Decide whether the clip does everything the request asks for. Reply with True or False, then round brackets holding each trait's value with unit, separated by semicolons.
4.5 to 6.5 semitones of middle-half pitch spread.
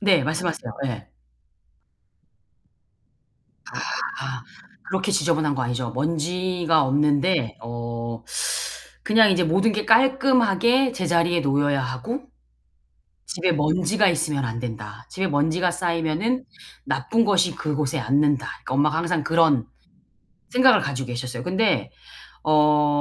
True (5.4 semitones)